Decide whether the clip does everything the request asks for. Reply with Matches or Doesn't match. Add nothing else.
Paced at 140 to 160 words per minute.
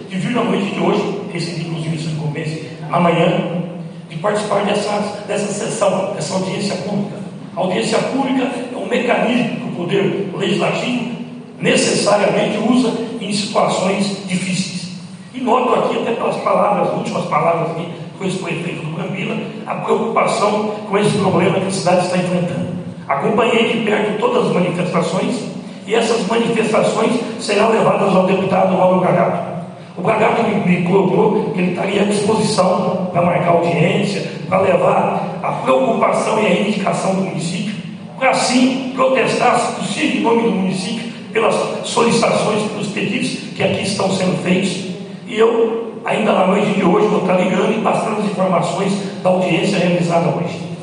Matches